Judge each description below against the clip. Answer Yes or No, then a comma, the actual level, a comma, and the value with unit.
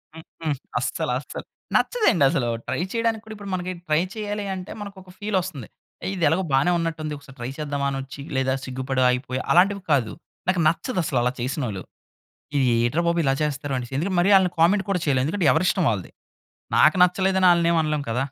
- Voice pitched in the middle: Yes, medium, 160 Hz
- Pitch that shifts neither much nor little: No, wide, 5.7 semitones